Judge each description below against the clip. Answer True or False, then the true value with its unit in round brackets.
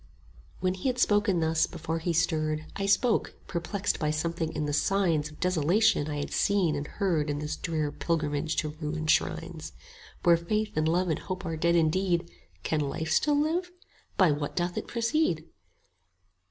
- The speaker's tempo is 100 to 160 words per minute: False (180 wpm)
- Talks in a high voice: False (165 Hz)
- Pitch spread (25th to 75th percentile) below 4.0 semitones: True (3.5 semitones)